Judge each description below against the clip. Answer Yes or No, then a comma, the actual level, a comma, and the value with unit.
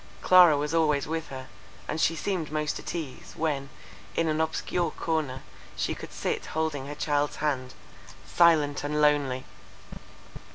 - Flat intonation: Yes, narrow, 2.0 semitones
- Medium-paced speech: Yes, average, 150 wpm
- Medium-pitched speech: Yes, medium, 150 Hz